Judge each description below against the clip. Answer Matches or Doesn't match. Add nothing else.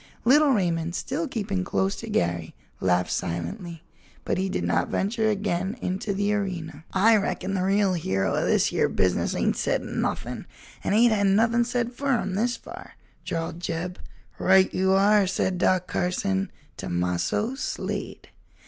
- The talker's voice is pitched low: Doesn't match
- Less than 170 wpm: Matches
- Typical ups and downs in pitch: Matches